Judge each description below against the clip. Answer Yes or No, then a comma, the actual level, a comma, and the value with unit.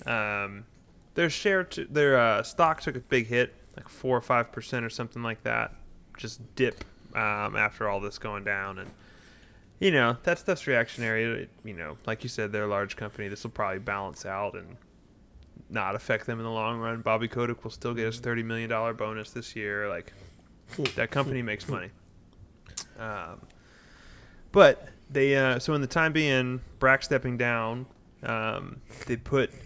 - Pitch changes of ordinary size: Yes, average, 3.6 semitones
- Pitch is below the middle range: Yes, low, 115 Hz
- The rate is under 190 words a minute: Yes, average, 180 wpm